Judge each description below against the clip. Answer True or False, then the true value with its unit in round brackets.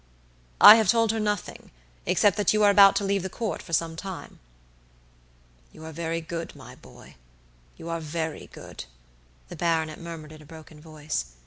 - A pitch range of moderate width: True (4.0 semitones)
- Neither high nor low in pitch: True (165 Hz)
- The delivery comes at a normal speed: True (180 wpm)